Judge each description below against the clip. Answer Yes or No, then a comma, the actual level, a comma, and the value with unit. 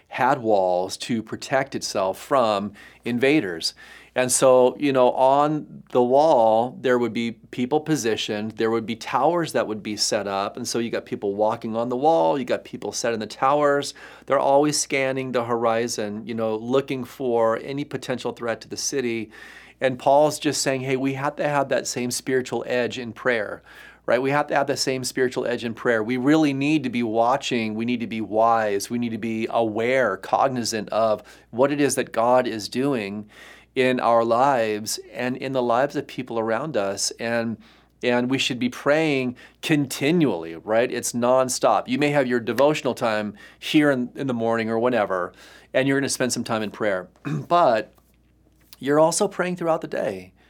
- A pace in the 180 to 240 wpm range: Yes, average, 190 wpm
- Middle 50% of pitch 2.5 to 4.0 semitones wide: Yes, average, 3.4 semitones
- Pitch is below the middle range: Yes, low, 125 Hz